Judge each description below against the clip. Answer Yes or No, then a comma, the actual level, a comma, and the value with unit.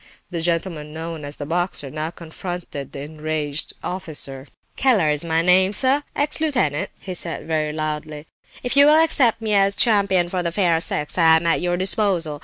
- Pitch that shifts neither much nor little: Yes, average, 4.2 semitones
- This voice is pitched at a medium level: Yes, medium, 170 Hz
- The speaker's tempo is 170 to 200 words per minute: Yes, average, 185 wpm